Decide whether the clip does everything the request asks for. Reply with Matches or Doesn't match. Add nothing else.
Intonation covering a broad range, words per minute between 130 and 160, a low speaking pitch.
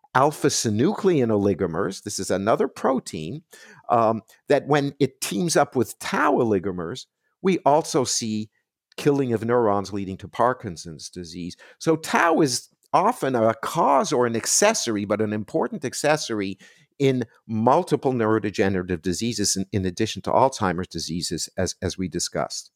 Matches